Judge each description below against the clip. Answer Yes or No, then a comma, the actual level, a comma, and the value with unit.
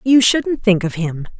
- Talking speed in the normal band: No, fast, 215 wpm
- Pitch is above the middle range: Yes, high, 210 Hz